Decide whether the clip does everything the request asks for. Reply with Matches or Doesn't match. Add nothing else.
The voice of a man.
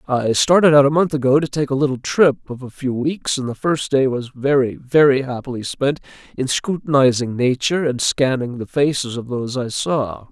Matches